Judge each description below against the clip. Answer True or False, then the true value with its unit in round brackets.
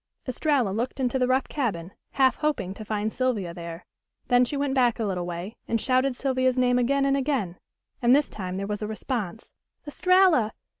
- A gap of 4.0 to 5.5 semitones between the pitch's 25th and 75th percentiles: True (4.5 semitones)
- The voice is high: True (245 Hz)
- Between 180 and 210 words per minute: True (190 wpm)